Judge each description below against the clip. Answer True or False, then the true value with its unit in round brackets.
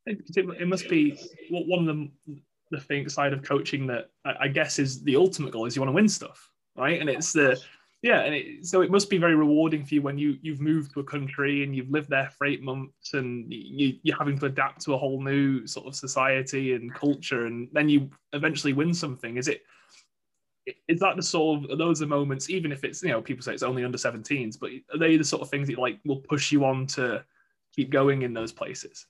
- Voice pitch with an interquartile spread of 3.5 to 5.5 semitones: False (2.8 semitones)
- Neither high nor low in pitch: True (145 Hz)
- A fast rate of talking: True (240 wpm)